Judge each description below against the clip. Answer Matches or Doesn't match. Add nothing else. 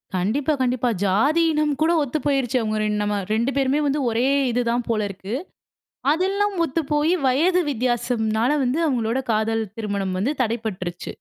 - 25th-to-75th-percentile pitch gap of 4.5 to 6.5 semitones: Matches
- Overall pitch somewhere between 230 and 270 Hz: Matches